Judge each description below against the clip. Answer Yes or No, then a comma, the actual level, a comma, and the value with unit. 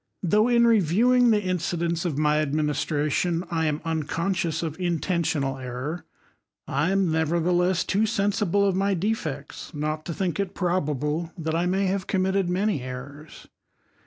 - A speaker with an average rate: Yes, average, 150 wpm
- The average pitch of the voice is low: No, medium, 170 Hz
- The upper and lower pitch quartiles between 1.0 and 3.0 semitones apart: No, average, 4.0 semitones